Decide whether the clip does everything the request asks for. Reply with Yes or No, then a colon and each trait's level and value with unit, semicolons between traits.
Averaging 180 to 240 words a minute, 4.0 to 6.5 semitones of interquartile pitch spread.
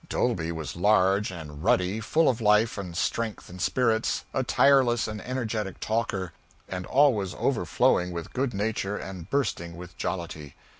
No: average, 150 wpm; average, 4.5 semitones